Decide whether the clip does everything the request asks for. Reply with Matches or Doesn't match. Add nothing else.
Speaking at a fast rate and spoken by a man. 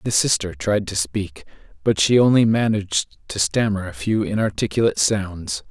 Doesn't match